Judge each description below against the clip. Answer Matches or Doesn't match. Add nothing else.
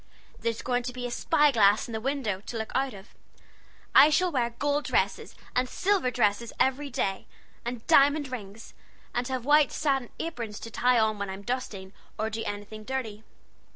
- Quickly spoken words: Doesn't match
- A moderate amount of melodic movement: Matches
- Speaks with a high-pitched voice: Matches